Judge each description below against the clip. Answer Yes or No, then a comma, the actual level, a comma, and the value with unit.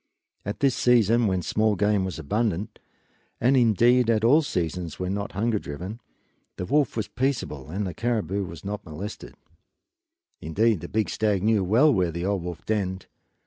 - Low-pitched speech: Yes, low, 105 Hz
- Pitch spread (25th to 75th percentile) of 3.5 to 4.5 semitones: Yes, average, 4.0 semitones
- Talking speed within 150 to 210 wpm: Yes, average, 175 wpm